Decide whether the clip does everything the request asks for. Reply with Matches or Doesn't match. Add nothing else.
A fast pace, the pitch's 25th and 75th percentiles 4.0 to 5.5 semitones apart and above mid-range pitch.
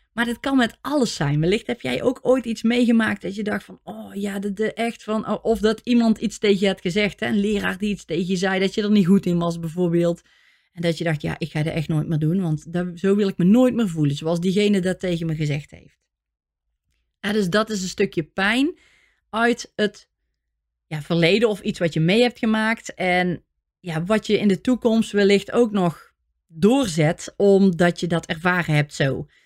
Matches